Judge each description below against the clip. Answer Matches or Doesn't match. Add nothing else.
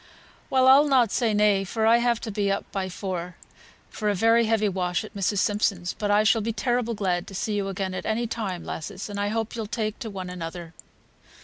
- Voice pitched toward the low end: Doesn't match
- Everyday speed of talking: Doesn't match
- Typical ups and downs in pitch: Matches